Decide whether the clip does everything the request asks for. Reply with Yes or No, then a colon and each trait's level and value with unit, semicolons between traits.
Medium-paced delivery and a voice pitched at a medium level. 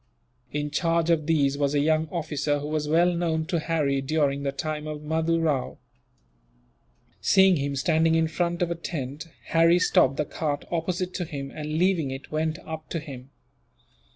Yes: average, 180 wpm; medium, 155 Hz